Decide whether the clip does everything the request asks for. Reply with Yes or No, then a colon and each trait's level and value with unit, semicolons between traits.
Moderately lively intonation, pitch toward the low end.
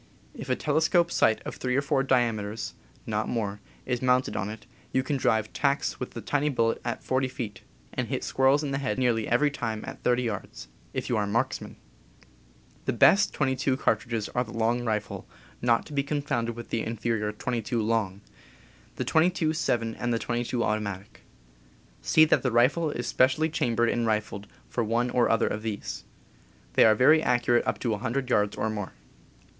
Yes: average, 3.1 semitones; low, 120 Hz